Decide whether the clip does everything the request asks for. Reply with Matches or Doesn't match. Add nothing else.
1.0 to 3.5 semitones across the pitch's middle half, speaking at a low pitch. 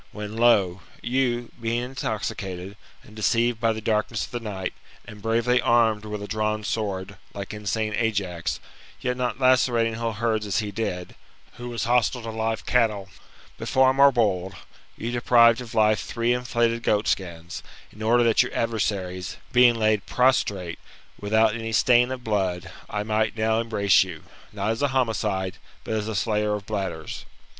Matches